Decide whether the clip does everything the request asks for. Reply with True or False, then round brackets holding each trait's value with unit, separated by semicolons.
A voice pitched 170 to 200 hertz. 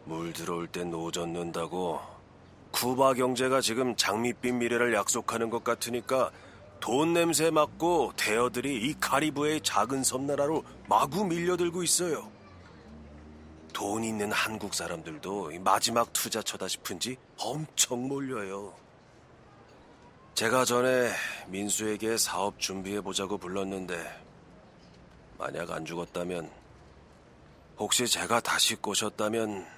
False (115 Hz)